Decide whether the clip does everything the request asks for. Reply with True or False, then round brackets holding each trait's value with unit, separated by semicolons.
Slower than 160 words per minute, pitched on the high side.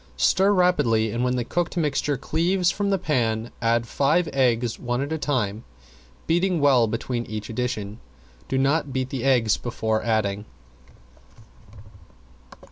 False (140 wpm; 125 Hz)